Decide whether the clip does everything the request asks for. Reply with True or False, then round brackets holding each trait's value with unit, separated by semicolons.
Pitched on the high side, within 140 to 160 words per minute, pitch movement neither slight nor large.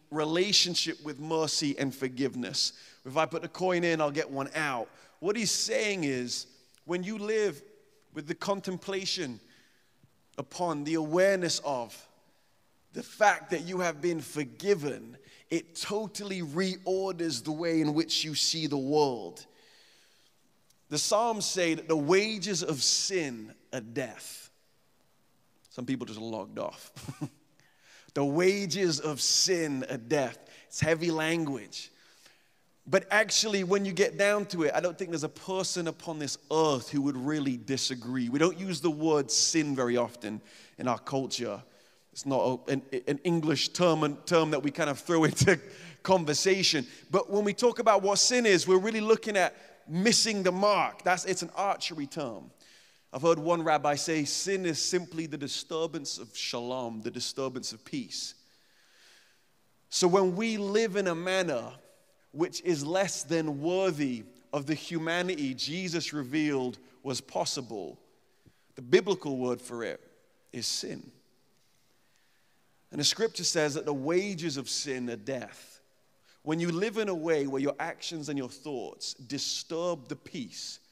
False (160 Hz; 150 wpm; 4.8 semitones)